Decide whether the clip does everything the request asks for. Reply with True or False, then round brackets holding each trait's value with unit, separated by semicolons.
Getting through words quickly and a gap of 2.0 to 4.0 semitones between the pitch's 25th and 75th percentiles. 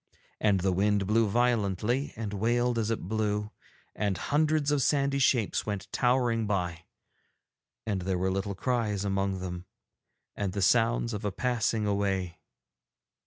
False (145 wpm; 3.6 semitones)